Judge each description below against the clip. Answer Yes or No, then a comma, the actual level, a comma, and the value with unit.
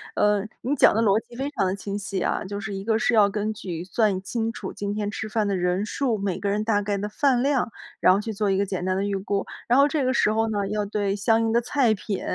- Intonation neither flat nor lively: No, narrow, 2.3 semitones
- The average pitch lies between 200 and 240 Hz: Yes, high, 210 Hz